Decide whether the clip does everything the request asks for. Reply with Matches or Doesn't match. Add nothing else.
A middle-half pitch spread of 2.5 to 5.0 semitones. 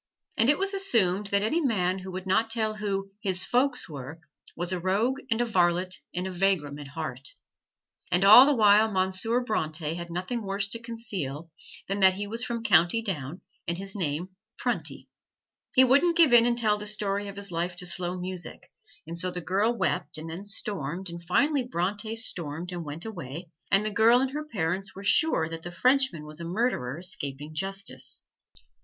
Matches